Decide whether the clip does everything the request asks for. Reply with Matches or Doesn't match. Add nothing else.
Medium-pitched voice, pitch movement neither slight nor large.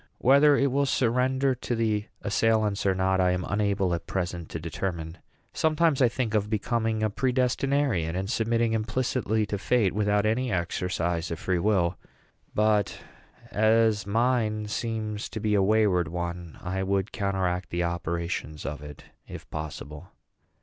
Doesn't match